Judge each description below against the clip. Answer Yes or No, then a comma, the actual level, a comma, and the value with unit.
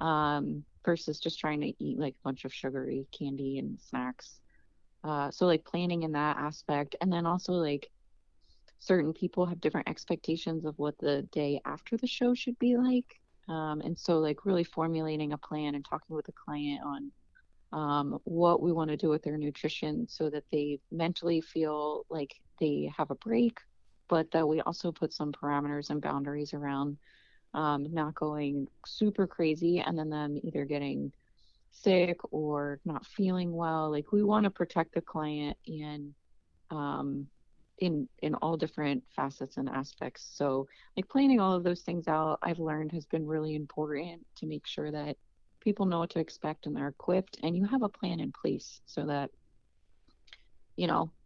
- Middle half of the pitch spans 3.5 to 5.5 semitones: No, average, 2.9 semitones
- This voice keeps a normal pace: Yes, average, 175 wpm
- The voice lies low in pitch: No, medium, 155 Hz